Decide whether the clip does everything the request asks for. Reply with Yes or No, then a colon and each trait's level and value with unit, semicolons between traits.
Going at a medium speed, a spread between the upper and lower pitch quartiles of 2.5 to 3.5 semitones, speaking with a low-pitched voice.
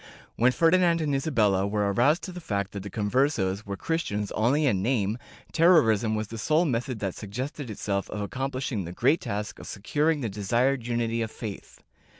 No: average, 185 wpm; wide, 5.5 semitones; low, 115 Hz